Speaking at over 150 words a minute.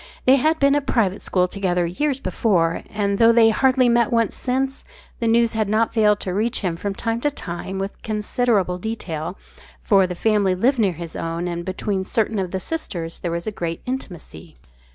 Yes: average, 200 wpm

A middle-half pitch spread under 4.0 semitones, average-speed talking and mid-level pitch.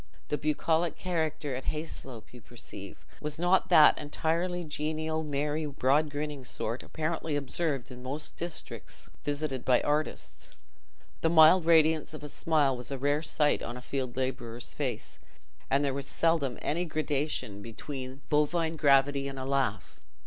Yes: average, 2.9 semitones; average, 155 wpm; medium, 150 Hz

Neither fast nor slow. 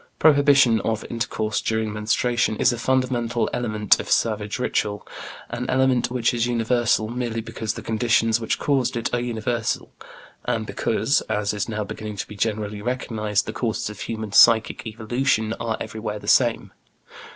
Yes: average, 160 wpm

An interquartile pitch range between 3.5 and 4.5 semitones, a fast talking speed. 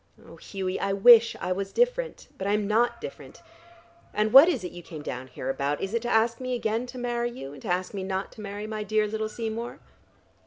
Yes: average, 4.0 semitones; fast, 235 wpm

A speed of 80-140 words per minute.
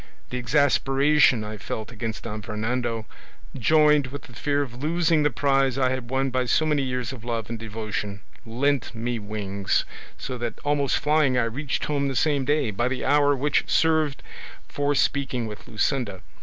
No: average, 175 wpm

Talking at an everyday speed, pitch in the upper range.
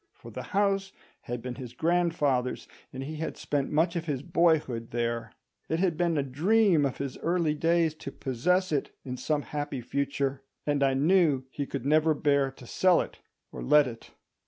No: average, 180 wpm; medium, 145 Hz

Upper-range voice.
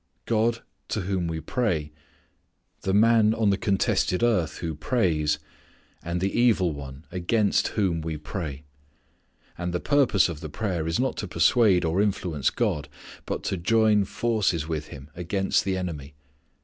No: very low, 90 Hz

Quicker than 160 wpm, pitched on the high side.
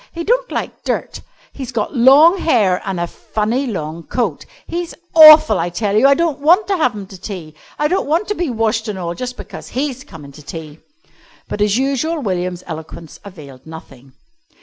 Yes: average, 195 wpm; high, 220 Hz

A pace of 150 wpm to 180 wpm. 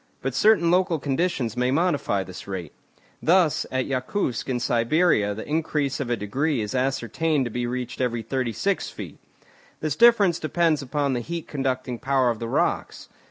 Yes: average, 165 wpm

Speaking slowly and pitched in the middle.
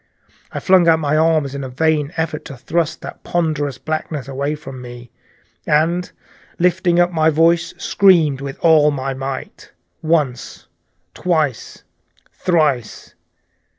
Yes: slow, 130 wpm; medium, 155 Hz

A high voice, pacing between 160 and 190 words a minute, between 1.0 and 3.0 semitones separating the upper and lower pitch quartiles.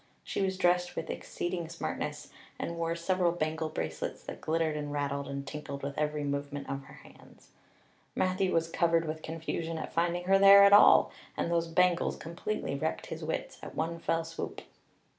No: medium, 165 Hz; average, 180 wpm; narrow, 2.4 semitones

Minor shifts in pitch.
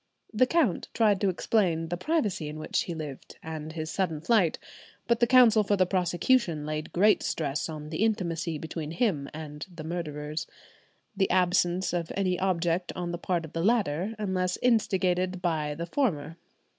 No: average, 3.9 semitones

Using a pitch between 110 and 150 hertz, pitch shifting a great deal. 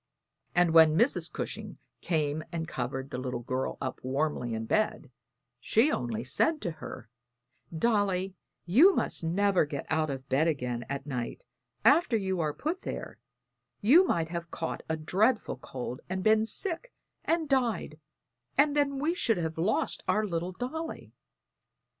No: medium, 170 Hz; wide, 8.3 semitones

